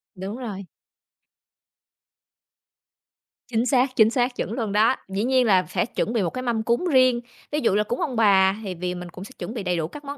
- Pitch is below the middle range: No, high, 225 Hz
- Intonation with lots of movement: No, average, 4.7 semitones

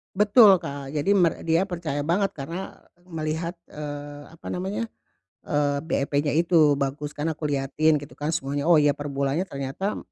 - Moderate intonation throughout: Yes, average, 3.1 semitones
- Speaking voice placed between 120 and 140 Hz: No, medium, 150 Hz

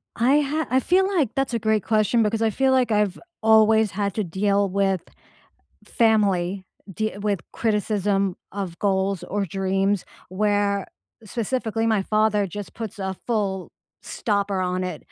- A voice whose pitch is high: Yes, high, 205 Hz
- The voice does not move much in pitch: Yes, narrow, 2.3 semitones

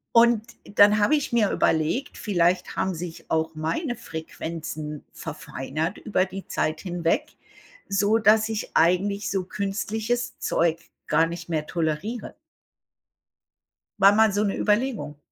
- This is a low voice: No, high, 195 Hz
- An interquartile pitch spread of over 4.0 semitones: Yes, average, 4.7 semitones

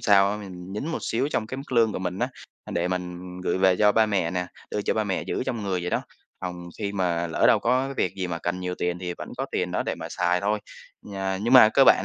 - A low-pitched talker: Yes, very low, 95 Hz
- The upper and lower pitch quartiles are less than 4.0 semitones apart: Yes, average, 3.3 semitones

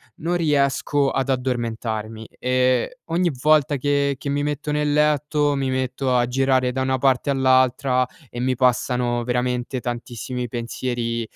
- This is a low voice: Yes, low, 130 Hz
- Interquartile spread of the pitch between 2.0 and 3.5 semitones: Yes, narrow, 2.5 semitones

